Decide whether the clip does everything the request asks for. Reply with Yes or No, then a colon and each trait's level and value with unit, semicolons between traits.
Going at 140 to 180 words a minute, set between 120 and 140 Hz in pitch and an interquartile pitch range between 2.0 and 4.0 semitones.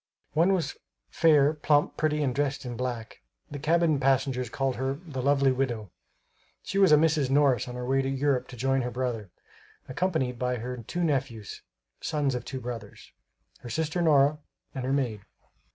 Yes: average, 175 wpm; low, 135 Hz; average, 3.1 semitones